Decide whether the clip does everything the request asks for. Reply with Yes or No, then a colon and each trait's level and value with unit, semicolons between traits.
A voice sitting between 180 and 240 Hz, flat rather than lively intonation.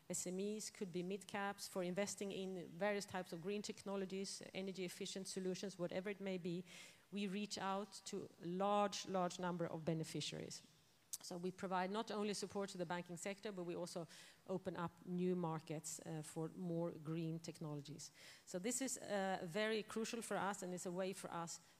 Yes: medium, 185 Hz; narrow, 2.3 semitones